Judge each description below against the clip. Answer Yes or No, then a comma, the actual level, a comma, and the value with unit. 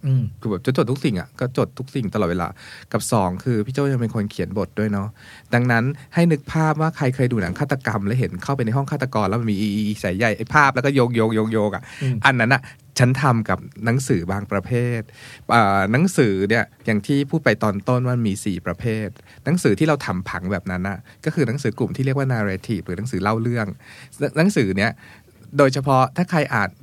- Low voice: Yes, low, 115 Hz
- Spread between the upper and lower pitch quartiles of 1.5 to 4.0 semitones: No, average, 4.4 semitones